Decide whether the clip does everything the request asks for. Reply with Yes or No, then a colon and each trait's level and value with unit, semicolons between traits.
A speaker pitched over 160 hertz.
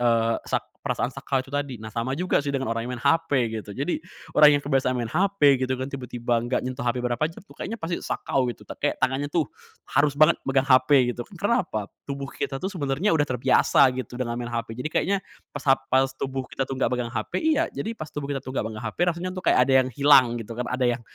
No: low, 135 Hz